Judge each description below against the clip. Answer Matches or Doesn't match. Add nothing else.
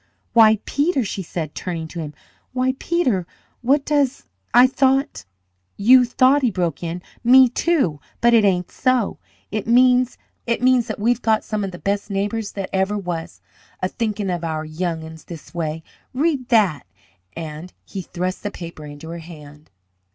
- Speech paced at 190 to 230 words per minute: Doesn't match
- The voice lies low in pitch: Doesn't match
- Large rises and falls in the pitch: Matches